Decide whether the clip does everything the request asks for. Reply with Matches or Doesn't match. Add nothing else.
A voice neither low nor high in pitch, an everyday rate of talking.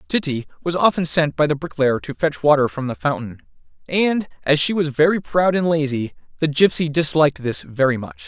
Matches